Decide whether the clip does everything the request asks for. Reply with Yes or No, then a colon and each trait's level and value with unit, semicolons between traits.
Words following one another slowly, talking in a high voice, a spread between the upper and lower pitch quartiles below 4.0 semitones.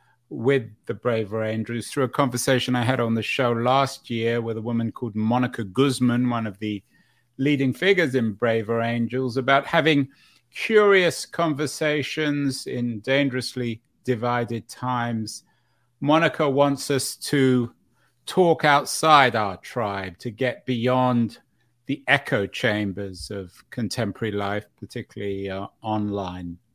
No: slow, 125 wpm; low, 120 Hz; average, 3.5 semitones